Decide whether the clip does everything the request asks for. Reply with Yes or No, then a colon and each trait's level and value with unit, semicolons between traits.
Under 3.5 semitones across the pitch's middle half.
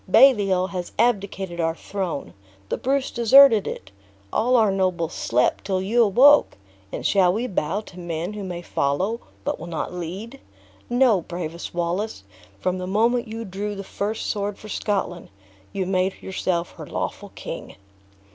No: average, 3.8 semitones